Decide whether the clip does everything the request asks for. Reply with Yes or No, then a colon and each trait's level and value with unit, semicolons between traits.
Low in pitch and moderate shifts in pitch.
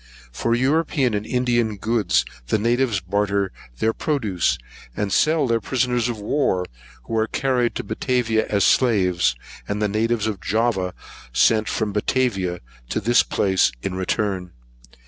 Yes: low, 110 Hz; average, 3.7 semitones